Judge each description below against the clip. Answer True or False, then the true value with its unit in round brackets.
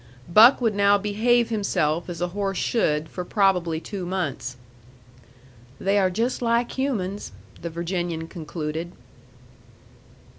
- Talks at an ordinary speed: False (120 wpm)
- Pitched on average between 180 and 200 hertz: True (190 Hz)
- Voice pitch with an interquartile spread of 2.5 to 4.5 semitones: True (3.7 semitones)